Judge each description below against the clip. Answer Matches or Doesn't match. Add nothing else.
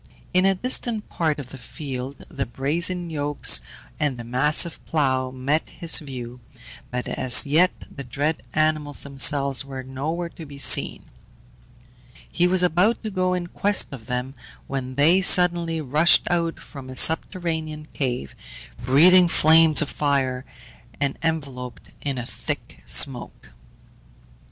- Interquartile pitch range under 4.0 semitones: Doesn't match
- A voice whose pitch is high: Doesn't match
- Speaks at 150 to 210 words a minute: Doesn't match